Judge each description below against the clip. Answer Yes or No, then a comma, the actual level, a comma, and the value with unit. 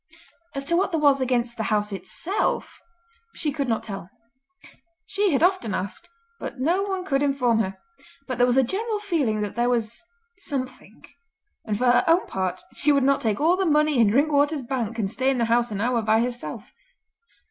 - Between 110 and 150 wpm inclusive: No, average, 195 wpm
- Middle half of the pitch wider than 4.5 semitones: Yes, average, 5.1 semitones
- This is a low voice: No, very high, 255 Hz